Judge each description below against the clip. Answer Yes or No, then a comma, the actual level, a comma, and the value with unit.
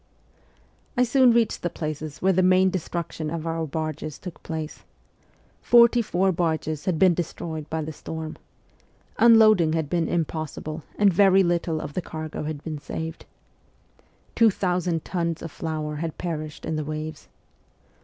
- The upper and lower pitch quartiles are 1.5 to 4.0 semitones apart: Yes, average, 2.8 semitones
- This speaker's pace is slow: No, average, 155 wpm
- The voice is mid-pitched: Yes, medium, 165 Hz